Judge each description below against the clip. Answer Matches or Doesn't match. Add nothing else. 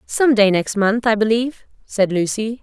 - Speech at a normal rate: Matches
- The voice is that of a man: Doesn't match